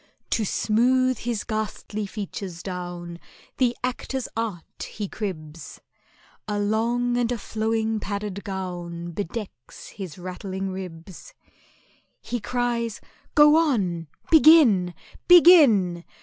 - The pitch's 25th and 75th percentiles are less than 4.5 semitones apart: No, average, 5.0 semitones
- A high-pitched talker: Yes, high, 210 Hz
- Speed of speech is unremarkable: No, slow, 100 wpm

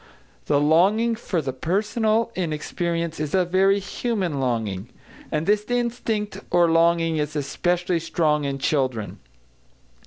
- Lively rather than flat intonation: No, average, 5.0 semitones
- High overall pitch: No, medium, 170 Hz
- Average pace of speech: No, slow, 130 wpm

